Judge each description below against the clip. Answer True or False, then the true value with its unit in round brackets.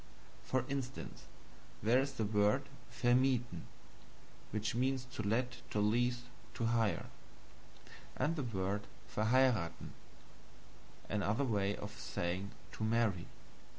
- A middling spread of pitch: True (3.5 semitones)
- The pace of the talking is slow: True (100 wpm)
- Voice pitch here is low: True (115 Hz)